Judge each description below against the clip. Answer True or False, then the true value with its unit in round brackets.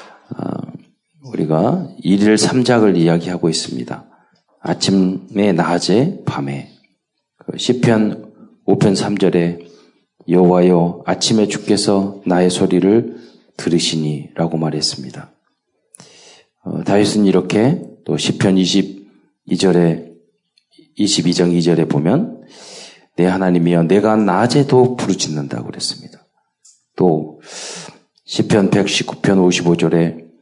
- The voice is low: True (90 Hz)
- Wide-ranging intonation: False (3.1 semitones)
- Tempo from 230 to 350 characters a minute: False (190 characters per minute)